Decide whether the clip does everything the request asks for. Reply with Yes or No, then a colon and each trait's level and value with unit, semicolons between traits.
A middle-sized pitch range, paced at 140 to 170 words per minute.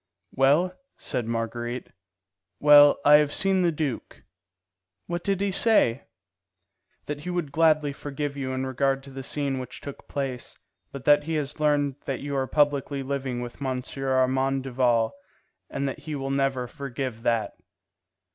No: narrow, 2.2 semitones; average, 155 wpm